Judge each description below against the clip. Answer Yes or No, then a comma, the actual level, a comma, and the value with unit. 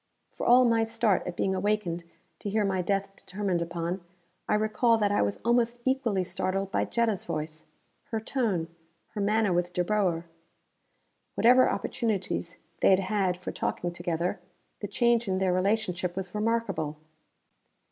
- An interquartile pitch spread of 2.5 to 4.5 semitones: Yes, average, 3.8 semitones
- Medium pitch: No, high, 195 Hz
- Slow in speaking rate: No, average, 155 wpm